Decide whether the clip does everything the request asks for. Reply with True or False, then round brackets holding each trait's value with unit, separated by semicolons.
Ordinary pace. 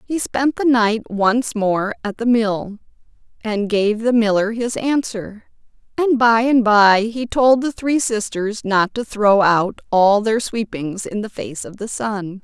True (180 wpm)